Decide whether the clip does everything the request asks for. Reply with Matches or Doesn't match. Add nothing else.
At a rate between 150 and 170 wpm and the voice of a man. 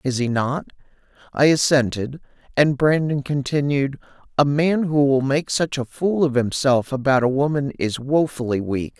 Matches